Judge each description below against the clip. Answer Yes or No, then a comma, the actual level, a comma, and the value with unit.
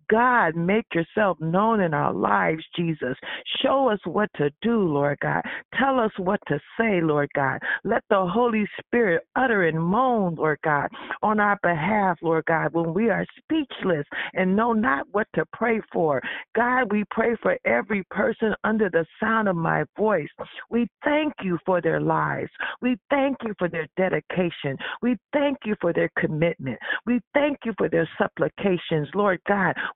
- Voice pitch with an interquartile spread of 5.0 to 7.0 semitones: Yes, wide, 5.6 semitones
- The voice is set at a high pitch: Yes, high, 200 Hz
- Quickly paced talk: No, average, 170 wpm